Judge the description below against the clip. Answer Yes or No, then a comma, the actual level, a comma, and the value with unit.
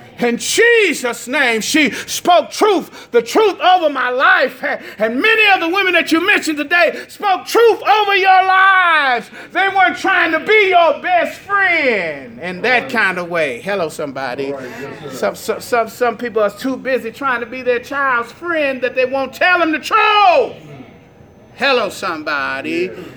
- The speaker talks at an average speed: Yes, average, 165 wpm